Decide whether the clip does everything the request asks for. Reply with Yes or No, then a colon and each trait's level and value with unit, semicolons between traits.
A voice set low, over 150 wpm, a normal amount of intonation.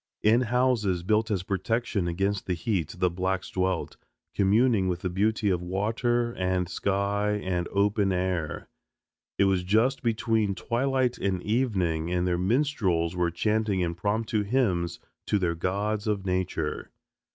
No: low, 100 Hz; average, 140 wpm; average, 3.5 semitones